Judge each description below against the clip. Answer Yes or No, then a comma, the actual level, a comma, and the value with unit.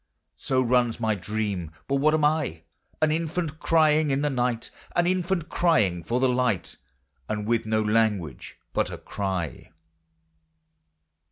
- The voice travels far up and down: Yes, wide, 6.4 semitones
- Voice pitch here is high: No, low, 125 Hz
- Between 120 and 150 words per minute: Yes, average, 145 wpm